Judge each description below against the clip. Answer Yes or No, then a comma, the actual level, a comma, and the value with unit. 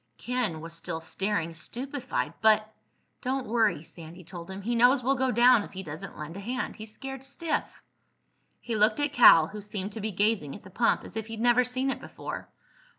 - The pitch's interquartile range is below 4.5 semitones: No, average, 5.0 semitones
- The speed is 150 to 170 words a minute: No, fast, 205 wpm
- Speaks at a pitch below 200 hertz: No, high, 220 Hz